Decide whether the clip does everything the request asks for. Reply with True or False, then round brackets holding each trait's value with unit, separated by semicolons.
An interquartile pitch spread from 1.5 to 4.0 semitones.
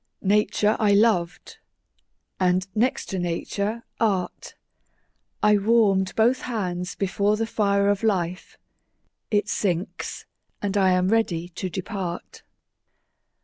True (2.8 semitones)